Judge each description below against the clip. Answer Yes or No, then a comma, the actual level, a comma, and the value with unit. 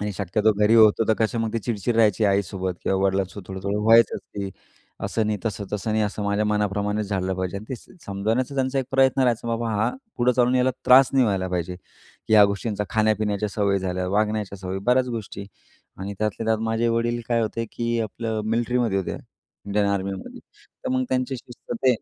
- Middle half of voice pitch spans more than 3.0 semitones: No, average, 2.7 semitones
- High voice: No, low, 105 Hz